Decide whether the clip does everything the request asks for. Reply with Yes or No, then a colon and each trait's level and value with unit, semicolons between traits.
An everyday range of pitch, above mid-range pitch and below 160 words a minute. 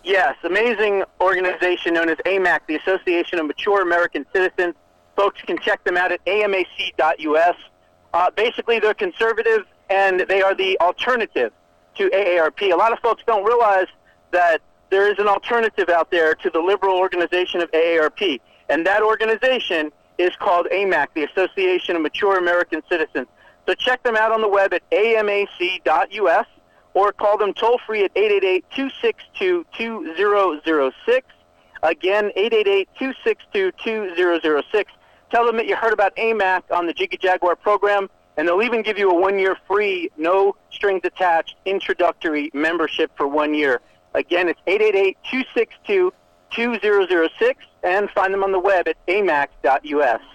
Yes: average, 4.7 semitones; high, 195 Hz; average, 140 wpm